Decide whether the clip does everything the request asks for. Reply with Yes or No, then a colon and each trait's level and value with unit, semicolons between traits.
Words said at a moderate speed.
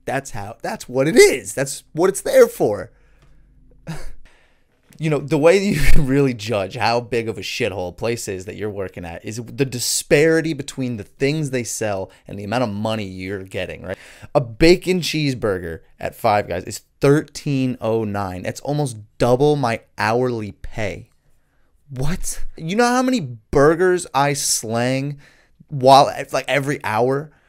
Yes: average, 160 wpm